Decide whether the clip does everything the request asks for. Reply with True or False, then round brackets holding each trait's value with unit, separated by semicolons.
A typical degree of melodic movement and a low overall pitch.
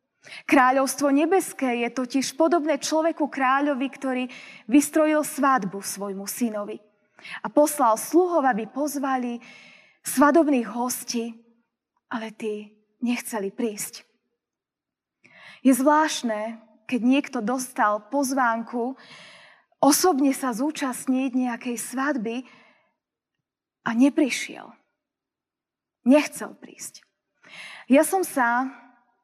False (3.7 semitones; 255 Hz)